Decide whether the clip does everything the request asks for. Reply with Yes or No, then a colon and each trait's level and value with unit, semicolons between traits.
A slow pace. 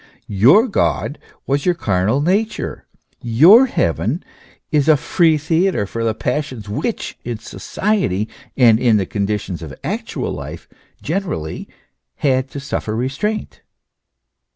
Yes: slow, 125 wpm